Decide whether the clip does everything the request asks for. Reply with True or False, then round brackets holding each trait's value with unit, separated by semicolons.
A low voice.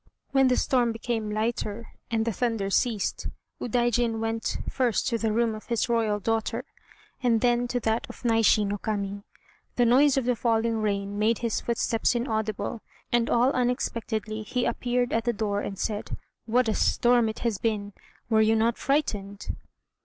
False (225 Hz)